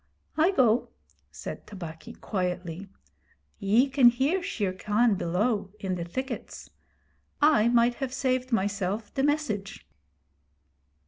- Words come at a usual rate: No, slow, 115 wpm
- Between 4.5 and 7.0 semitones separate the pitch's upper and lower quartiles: Yes, average, 5.0 semitones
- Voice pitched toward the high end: Yes, high, 225 Hz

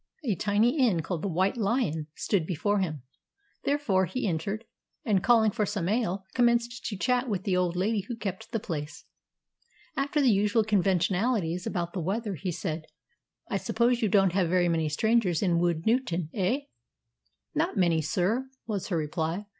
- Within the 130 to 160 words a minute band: No, average, 170 wpm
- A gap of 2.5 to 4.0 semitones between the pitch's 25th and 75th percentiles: No, average, 4.7 semitones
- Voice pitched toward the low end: No, high, 195 Hz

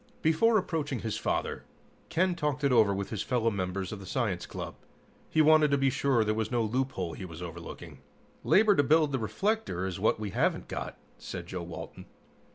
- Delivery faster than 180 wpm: Yes, average, 195 wpm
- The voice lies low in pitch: Yes, low, 125 Hz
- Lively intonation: Yes, wide, 7.4 semitones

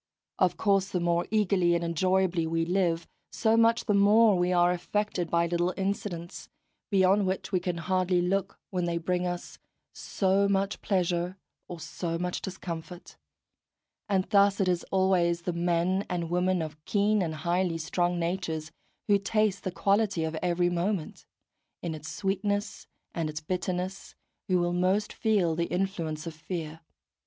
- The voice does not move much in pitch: Yes, narrow, 2.3 semitones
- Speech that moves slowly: No, average, 160 wpm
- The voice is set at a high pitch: No, medium, 180 Hz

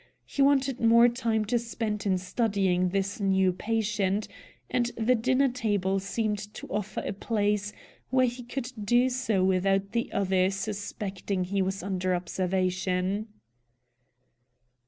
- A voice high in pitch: Yes, high, 205 Hz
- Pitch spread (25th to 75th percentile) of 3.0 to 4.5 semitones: Yes, average, 3.5 semitones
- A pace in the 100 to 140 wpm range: Yes, slow, 135 wpm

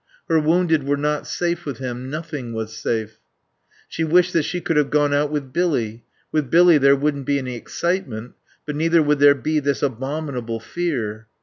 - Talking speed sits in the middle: Yes, average, 185 wpm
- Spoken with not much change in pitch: No, average, 3.9 semitones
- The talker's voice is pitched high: No, medium, 145 Hz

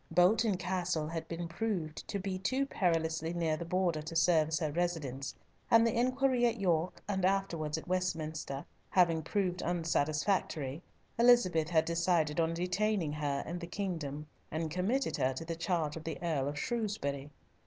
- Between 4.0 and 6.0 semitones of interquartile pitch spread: No, average, 3.2 semitones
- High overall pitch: No, medium, 170 Hz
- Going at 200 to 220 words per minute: No, average, 165 wpm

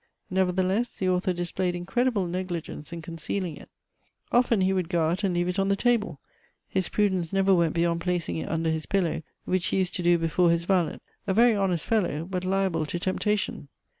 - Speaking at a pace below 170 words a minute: No, average, 195 wpm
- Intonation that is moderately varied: No, narrow, 2.3 semitones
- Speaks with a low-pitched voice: No, medium, 180 Hz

